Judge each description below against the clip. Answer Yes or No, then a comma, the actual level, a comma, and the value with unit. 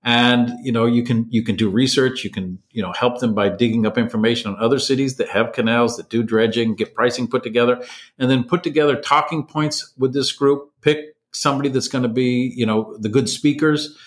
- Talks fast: Yes, fast, 220 wpm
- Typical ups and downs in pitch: Yes, average, 3.2 semitones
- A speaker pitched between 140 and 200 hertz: No, low, 125 Hz